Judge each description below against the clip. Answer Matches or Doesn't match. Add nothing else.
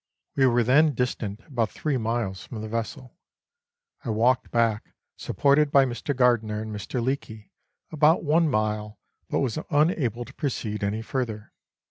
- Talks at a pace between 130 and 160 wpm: Matches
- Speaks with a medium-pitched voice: Doesn't match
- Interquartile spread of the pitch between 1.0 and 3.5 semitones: Doesn't match